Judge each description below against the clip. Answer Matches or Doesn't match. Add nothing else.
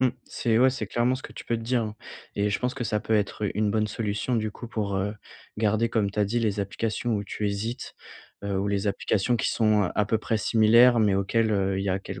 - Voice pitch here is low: Matches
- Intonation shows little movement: Matches